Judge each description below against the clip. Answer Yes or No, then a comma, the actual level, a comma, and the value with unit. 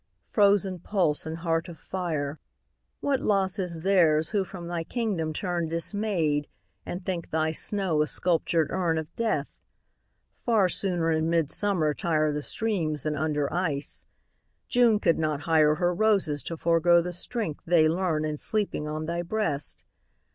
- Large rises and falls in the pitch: No, average, 3.5 semitones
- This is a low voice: No, medium, 170 Hz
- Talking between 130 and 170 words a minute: Yes, average, 155 wpm